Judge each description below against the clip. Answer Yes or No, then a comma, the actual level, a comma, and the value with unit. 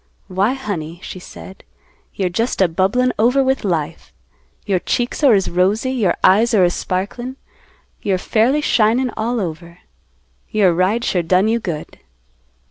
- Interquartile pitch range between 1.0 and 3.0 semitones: No, average, 4.7 semitones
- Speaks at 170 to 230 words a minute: No, average, 150 wpm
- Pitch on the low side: No, high, 200 Hz